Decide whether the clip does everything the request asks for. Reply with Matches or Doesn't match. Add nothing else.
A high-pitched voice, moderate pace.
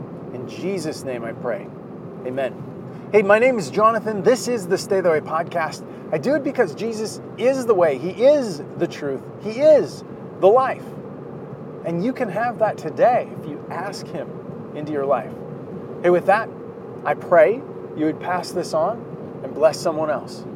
Matches